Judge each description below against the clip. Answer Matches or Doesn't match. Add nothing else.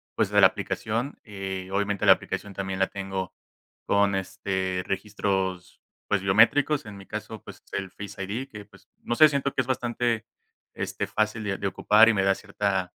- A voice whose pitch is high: Doesn't match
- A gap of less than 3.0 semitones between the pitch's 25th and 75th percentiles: Matches